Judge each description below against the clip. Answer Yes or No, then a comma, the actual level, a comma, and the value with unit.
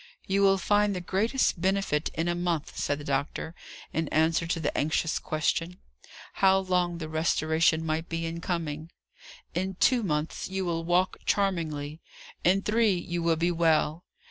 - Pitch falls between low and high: Yes, medium, 170 Hz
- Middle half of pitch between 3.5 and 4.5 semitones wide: No, average, 2.9 semitones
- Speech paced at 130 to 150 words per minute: No, average, 165 wpm